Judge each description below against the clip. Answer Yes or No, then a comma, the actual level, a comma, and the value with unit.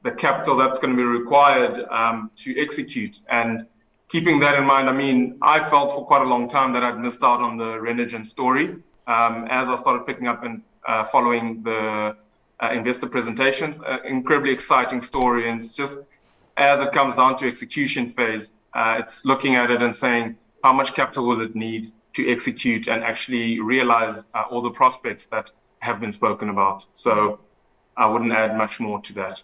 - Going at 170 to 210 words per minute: Yes, average, 190 wpm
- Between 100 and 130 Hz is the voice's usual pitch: Yes, low, 120 Hz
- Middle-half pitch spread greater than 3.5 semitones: No, average, 2.9 semitones